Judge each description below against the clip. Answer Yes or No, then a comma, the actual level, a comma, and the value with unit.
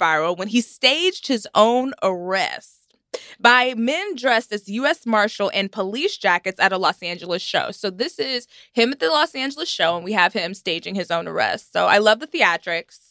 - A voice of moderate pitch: No, high, 215 Hz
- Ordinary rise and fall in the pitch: No, wide, 5.7 semitones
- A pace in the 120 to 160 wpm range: No, average, 190 wpm